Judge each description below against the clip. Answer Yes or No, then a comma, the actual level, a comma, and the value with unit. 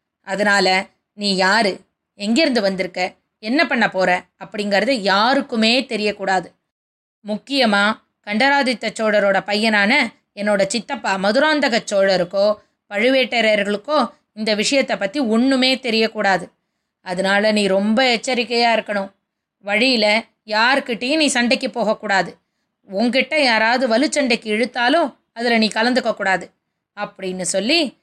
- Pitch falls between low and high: No, high, 220 Hz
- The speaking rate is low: No, average, 95 wpm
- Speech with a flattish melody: No, average, 4.2 semitones